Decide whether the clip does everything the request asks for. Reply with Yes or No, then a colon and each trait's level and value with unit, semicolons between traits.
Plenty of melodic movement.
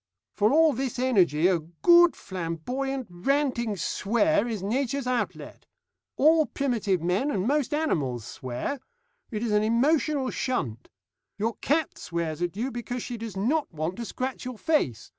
Yes: wide, 7.2 semitones